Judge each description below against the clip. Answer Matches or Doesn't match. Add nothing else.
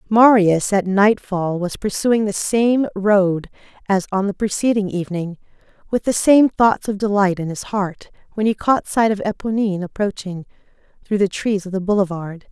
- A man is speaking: Doesn't match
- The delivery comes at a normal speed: Matches